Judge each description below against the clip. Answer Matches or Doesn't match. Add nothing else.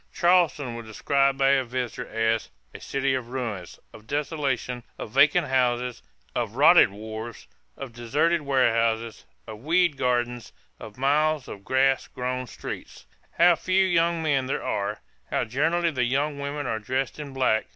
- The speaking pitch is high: Doesn't match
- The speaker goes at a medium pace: Matches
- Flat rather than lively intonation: Doesn't match